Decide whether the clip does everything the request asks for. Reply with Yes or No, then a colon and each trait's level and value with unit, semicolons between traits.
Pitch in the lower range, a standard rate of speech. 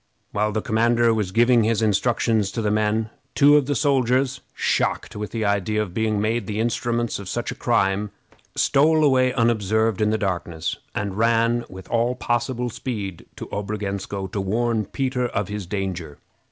Yes: low, 110 Hz; average, 170 wpm